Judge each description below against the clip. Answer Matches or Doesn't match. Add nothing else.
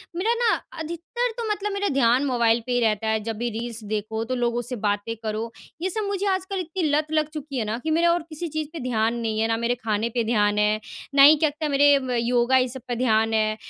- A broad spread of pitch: Matches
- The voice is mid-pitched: Doesn't match